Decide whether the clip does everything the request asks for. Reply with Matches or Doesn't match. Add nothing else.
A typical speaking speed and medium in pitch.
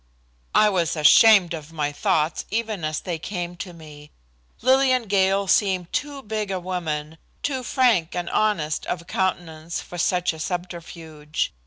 Matches